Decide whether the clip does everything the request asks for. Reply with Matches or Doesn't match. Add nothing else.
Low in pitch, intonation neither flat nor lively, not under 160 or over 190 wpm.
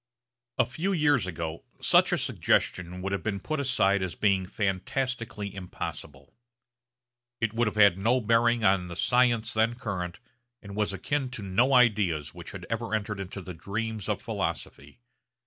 Matches